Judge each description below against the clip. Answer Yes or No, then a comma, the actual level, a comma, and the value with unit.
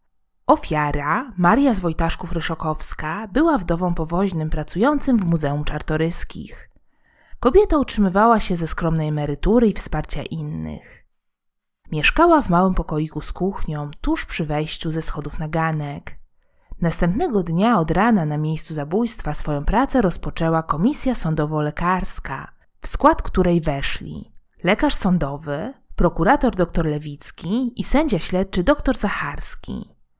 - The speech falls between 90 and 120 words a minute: Yes, average, 115 wpm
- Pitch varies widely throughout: Yes, wide, 5.9 semitones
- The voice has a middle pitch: Yes, medium, 170 Hz